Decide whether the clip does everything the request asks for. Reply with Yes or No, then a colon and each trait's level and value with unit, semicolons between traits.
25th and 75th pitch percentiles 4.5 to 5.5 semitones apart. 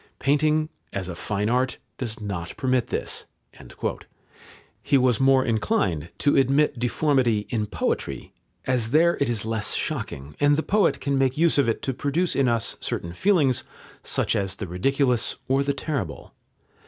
Yes: average, 4.9 semitones